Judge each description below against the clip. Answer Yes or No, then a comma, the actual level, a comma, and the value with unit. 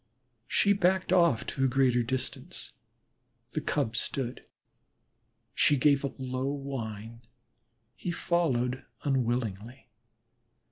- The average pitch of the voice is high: No, low, 130 Hz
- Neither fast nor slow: No, slow, 100 wpm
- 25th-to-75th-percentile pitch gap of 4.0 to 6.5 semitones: No, average, 3.4 semitones